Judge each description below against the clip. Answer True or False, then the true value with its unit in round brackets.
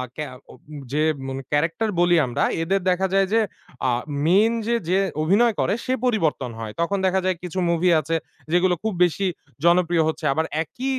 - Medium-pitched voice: True (180 Hz)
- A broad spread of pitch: False (3.6 semitones)